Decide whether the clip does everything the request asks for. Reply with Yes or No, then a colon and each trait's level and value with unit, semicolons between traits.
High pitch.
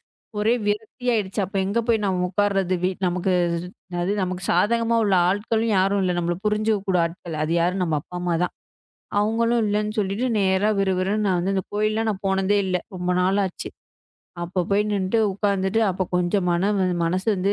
Yes: high, 195 Hz